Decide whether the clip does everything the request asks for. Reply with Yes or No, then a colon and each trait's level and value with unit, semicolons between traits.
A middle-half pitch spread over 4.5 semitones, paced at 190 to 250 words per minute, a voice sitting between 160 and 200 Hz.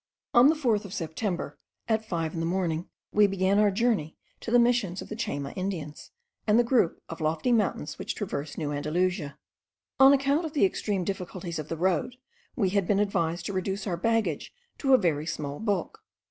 Yes: average, 5.1 semitones; average, 195 wpm; high, 190 Hz